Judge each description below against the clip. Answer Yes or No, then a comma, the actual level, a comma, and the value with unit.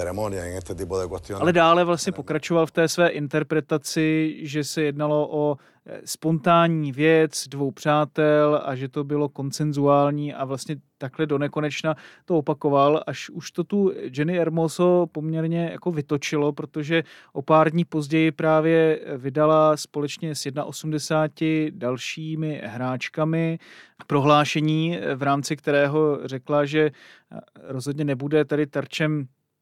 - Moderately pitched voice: Yes, medium, 150 Hz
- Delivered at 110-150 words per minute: Yes, average, 120 wpm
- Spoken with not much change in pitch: Yes, narrow, 1.9 semitones